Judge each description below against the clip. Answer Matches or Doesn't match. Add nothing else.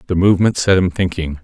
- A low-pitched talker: Matches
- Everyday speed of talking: Doesn't match